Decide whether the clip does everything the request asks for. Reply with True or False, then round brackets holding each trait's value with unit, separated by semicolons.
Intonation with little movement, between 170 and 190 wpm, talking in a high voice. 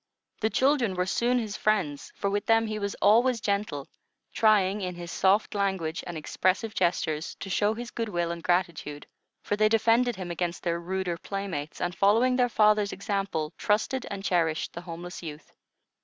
False (3.8 semitones; 175 wpm; 195 Hz)